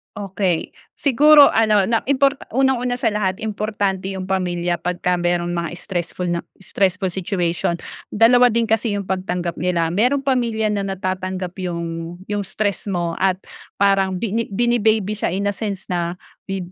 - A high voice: Yes, high, 195 Hz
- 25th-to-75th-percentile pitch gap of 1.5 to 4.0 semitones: Yes, average, 3.5 semitones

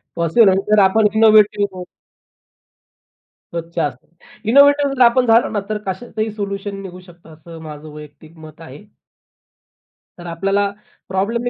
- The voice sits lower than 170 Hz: No, high, 195 Hz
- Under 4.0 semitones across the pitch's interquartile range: No, average, 4.6 semitones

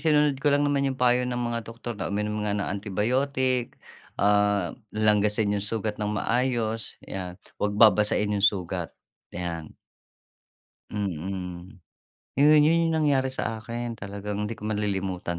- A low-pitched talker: Yes, low, 105 Hz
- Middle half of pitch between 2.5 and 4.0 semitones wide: Yes, average, 3.7 semitones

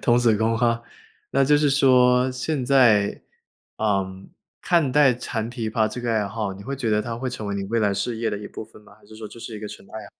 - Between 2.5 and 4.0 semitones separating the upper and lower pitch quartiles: Yes, average, 2.9 semitones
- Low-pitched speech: Yes, low, 115 Hz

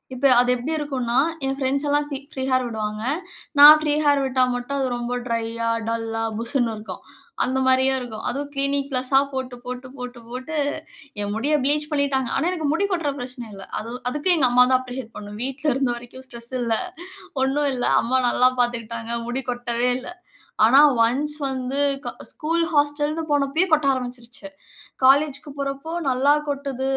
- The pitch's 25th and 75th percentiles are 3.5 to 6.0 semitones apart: No, average, 2.8 semitones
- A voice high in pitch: Yes, very high, 260 Hz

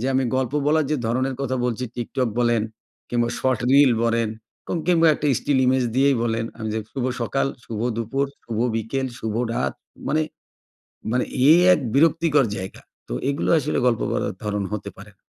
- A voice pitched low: Yes, low, 125 Hz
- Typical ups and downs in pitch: Yes, average, 3.4 semitones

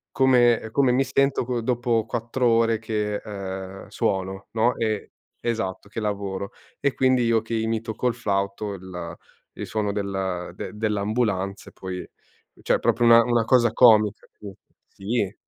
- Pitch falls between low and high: No, low, 110 Hz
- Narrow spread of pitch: No, average, 3.2 semitones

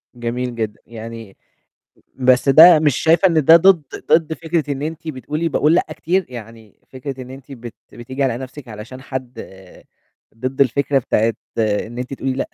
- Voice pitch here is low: Yes, low, 130 Hz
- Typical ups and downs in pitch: Yes, average, 4.4 semitones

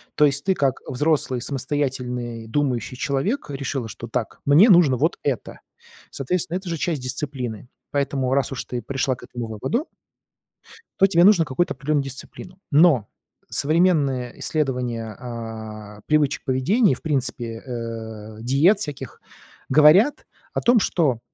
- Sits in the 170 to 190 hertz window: No, low, 135 Hz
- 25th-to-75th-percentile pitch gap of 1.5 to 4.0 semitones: No, average, 4.4 semitones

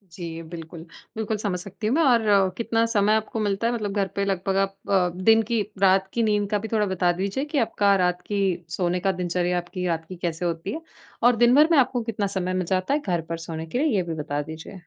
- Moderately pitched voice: No, high, 195 Hz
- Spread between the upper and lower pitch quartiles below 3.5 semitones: No, average, 3.9 semitones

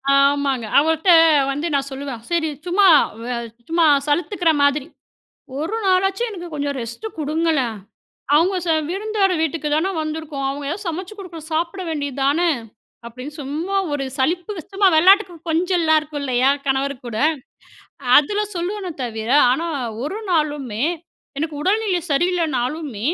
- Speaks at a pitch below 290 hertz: No, very high, 315 Hz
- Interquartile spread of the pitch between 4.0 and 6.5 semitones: Yes, average, 4.4 semitones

